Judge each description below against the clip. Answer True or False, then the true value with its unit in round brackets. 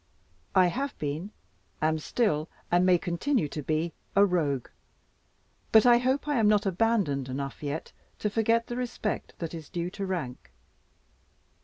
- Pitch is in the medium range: True (180 Hz)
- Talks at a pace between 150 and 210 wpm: True (155 wpm)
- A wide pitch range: True (6.5 semitones)